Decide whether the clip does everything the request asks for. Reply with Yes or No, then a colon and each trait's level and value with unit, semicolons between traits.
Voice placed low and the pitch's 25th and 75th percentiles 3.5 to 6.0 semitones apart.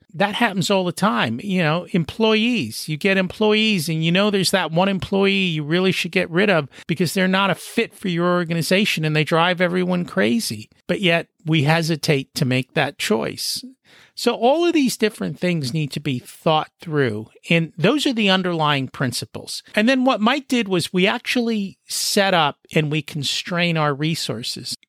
No: medium, 180 Hz; average, 4.3 semitones